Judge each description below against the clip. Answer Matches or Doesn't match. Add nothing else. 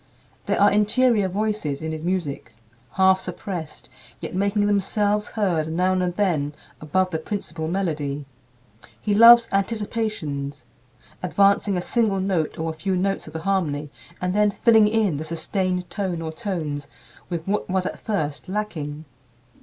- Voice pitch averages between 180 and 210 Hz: Matches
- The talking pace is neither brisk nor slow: Matches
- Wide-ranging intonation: Doesn't match